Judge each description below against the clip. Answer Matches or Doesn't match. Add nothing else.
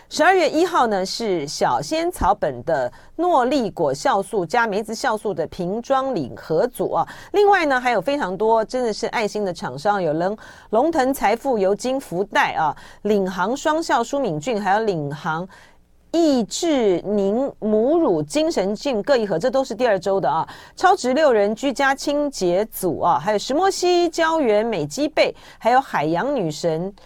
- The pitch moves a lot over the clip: Matches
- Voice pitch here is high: Matches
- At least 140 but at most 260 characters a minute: Matches